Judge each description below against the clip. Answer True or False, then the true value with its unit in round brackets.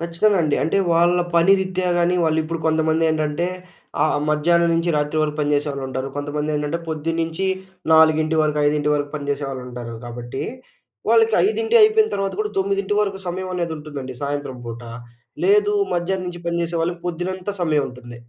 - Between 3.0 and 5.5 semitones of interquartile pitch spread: True (3.3 semitones)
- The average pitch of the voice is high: False (160 Hz)